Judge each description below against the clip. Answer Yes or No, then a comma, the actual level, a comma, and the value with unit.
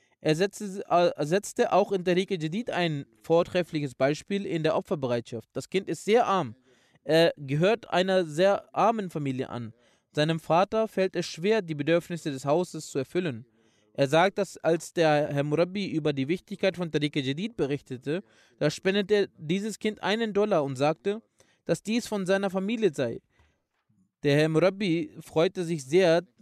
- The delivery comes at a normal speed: Yes, average, 155 wpm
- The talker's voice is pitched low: No, medium, 170 Hz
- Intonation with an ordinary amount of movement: Yes, average, 4.8 semitones